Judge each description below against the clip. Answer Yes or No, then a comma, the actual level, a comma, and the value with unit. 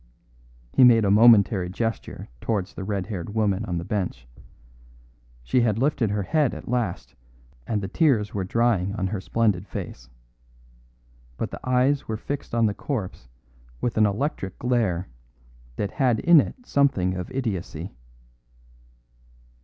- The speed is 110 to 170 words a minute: Yes, average, 145 wpm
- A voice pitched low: Yes, low, 105 Hz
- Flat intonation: No, average, 4.3 semitones